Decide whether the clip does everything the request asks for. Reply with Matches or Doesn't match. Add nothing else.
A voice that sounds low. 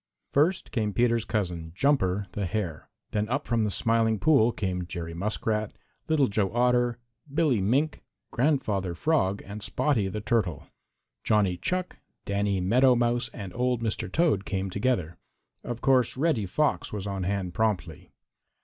Matches